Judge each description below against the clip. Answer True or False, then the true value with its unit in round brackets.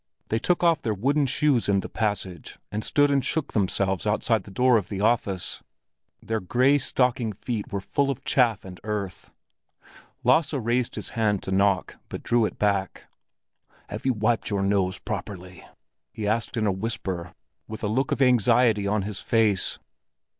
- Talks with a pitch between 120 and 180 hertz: False (110 Hz)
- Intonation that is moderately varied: True (3.9 semitones)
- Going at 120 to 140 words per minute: False (175 wpm)